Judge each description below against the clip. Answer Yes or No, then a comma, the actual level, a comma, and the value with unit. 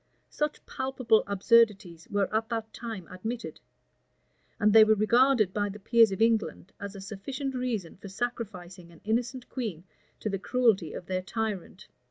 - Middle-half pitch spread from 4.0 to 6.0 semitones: No, average, 3.4 semitones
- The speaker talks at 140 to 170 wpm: Yes, average, 160 wpm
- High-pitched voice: Yes, high, 215 Hz